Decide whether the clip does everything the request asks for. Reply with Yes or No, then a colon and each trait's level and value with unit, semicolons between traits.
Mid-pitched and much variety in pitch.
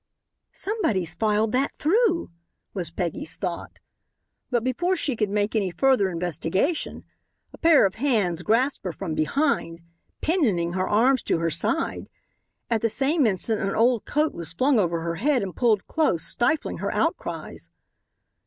No: high, 220 Hz; wide, 7.6 semitones